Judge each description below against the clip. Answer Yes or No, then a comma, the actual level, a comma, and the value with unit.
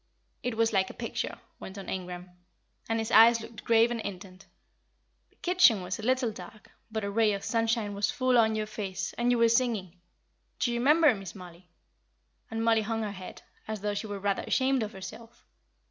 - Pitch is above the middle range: Yes, high, 220 Hz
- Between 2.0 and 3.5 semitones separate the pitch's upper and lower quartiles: Yes, average, 2.9 semitones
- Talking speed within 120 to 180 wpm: No, average, 200 wpm